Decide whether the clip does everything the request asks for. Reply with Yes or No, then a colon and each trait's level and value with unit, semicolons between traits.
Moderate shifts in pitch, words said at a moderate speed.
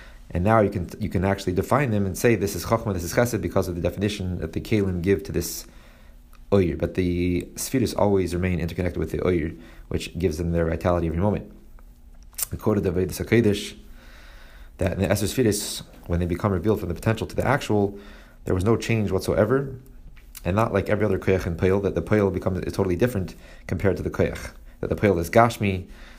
No: average, 3.3 semitones; fast, 210 wpm